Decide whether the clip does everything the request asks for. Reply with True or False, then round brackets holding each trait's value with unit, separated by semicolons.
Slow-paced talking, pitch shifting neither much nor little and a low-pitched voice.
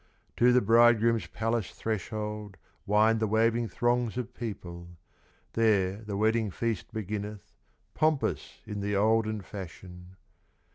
False (115 wpm; 2.3 semitones; 110 Hz)